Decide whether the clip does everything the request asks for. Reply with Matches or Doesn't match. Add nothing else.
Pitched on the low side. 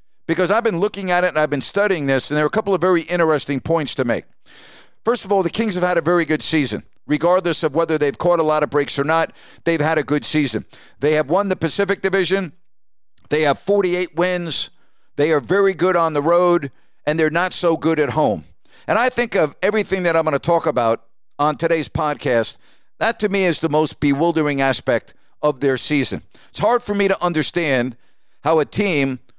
Doesn't match